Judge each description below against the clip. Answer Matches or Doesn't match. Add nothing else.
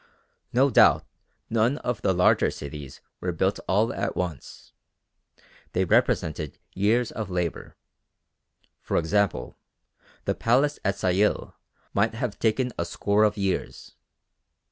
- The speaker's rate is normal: Doesn't match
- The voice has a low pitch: Matches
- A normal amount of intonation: Matches